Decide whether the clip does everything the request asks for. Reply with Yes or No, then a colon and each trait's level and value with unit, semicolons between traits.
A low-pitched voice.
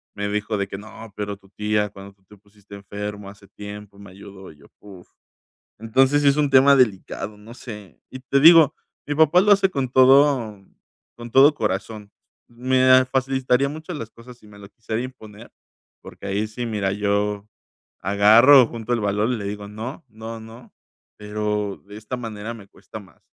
Yes: low, 110 Hz